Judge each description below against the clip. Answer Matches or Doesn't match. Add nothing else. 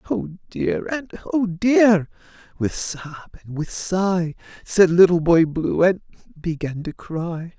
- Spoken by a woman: Doesn't match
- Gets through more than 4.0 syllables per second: Doesn't match